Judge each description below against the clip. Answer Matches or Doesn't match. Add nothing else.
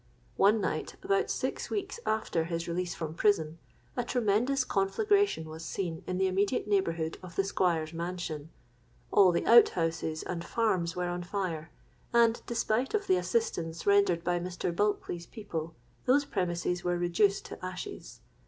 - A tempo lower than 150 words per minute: Doesn't match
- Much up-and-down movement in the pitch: Doesn't match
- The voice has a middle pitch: Matches